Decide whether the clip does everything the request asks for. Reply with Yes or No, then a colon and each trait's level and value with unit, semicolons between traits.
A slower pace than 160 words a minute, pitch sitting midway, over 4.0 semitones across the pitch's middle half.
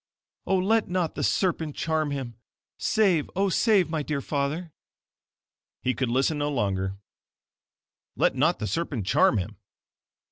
Yes: average, 140 wpm; medium, 150 Hz; wide, 5.4 semitones